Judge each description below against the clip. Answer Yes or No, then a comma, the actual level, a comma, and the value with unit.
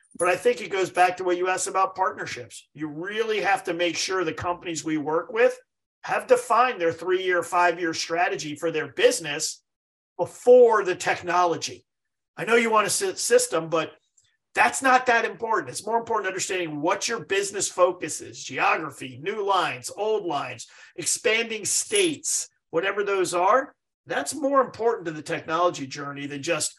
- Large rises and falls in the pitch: Yes, wide, 6.0 semitones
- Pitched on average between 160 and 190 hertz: Yes, medium, 185 Hz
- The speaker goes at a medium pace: Yes, average, 175 wpm